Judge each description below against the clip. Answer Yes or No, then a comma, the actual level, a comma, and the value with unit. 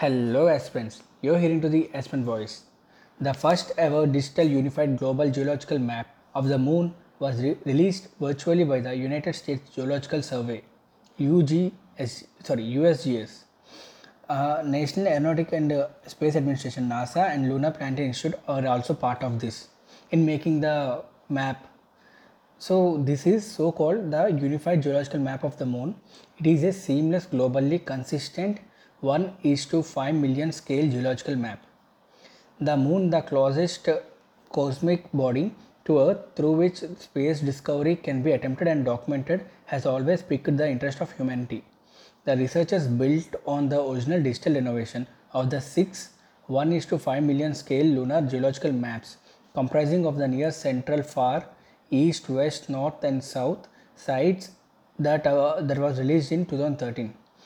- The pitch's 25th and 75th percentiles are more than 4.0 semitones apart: No, average, 3.6 semitones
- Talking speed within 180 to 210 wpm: No, average, 145 wpm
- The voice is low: No, medium, 145 Hz